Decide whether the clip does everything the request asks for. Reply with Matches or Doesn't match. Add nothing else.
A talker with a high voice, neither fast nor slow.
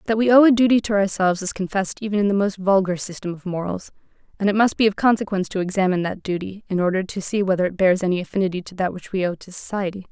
Doesn't match